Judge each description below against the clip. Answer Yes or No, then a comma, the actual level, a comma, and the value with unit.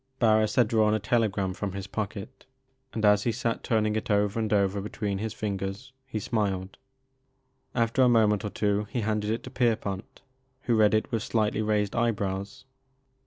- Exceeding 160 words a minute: Yes, average, 175 wpm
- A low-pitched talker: Yes, low, 105 Hz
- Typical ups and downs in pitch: No, narrow, 1.9 semitones